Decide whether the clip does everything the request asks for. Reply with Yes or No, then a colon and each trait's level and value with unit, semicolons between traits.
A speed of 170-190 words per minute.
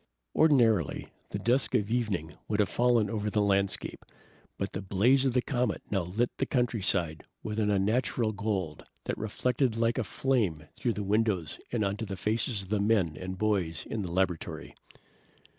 Yes: average, 175 wpm